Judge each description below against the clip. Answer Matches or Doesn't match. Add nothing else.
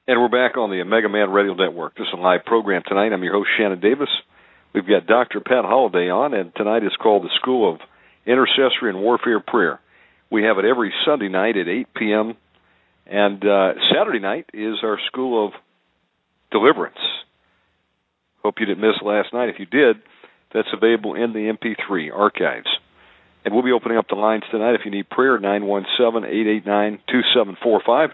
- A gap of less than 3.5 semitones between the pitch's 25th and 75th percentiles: Matches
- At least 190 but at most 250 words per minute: Doesn't match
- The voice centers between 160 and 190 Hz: Doesn't match